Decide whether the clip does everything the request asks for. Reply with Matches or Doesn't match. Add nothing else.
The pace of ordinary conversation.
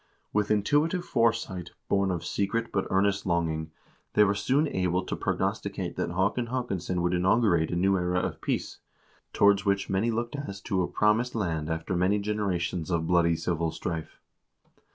Matches